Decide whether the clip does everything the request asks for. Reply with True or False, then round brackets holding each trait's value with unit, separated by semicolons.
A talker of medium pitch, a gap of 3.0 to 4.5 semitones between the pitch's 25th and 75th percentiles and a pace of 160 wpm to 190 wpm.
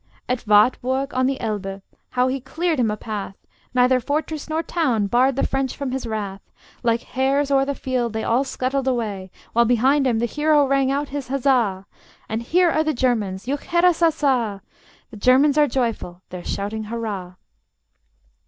False (255 Hz; 3.9 semitones; 170 wpm)